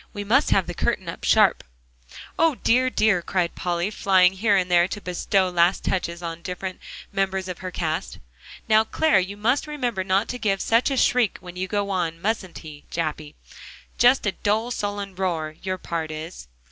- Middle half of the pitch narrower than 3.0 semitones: No, average, 3.4 semitones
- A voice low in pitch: No, high, 190 Hz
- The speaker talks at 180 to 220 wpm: Yes, average, 190 wpm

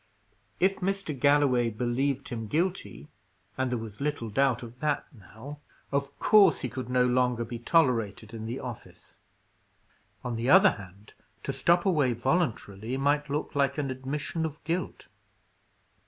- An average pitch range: Yes, average, 4.1 semitones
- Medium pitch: No, low, 130 Hz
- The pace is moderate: Yes, average, 150 wpm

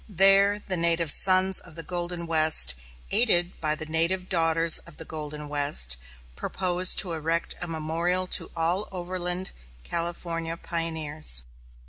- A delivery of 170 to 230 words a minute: No, slow, 135 wpm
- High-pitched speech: No, medium, 170 Hz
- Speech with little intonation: Yes, narrow, 2.2 semitones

